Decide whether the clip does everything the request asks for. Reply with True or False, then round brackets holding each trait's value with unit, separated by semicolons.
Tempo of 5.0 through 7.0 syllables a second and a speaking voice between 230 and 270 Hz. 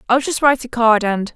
True (6.0 syllables/s; 240 Hz)